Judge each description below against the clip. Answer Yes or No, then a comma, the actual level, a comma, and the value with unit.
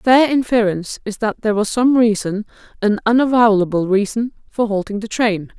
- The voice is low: No, high, 220 Hz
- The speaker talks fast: No, average, 170 wpm